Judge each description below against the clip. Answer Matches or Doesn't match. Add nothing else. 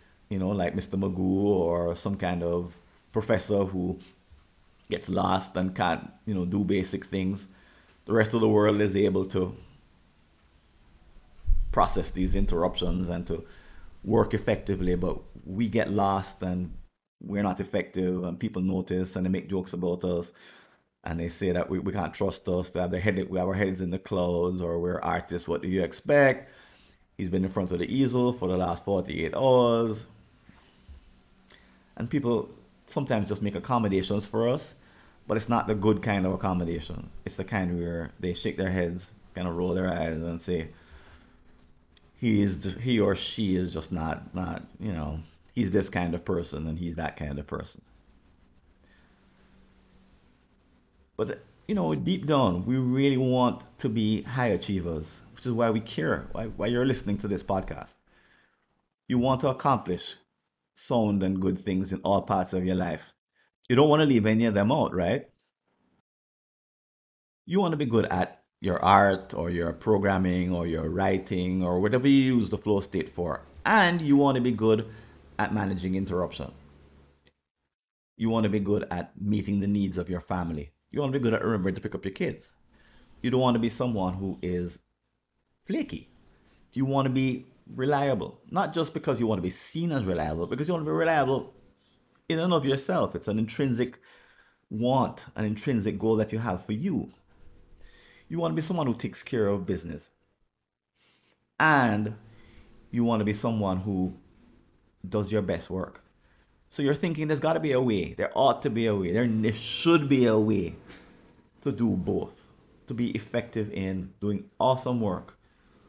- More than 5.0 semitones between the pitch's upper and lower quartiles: Doesn't match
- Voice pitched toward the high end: Doesn't match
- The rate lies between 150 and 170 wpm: Doesn't match